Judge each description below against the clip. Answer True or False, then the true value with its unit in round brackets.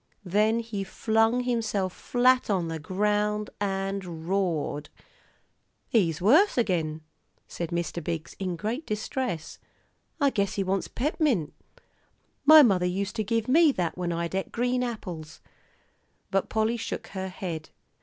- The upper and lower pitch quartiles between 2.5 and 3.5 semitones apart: False (4.7 semitones)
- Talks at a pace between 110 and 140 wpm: True (135 wpm)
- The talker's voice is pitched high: True (200 Hz)